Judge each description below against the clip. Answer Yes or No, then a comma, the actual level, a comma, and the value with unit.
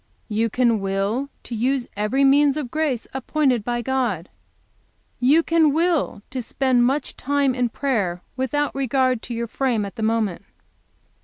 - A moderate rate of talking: Yes, average, 155 wpm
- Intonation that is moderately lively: Yes, average, 3.6 semitones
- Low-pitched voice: No, very high, 255 Hz